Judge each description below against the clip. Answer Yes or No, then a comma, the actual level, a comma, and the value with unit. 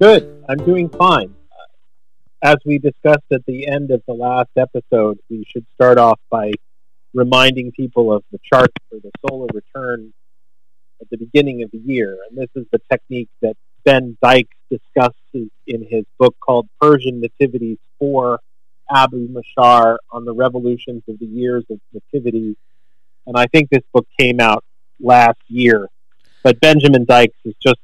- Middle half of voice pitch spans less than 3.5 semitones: Yes, narrow, 2.4 semitones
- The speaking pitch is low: Yes, low, 125 Hz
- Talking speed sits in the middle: Yes, average, 160 wpm